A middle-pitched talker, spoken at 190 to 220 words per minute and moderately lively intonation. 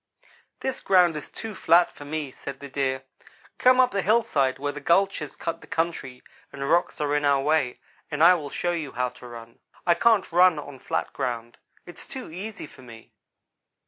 Yes: medium, 150 Hz; average, 195 wpm; average, 4.7 semitones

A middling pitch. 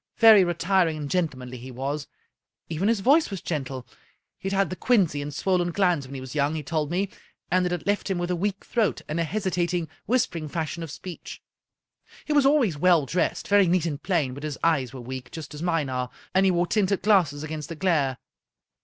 Yes: medium, 170 Hz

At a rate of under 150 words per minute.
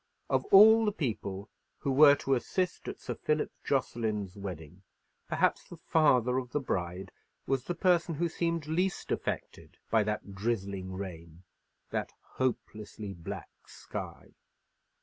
Yes: slow, 135 wpm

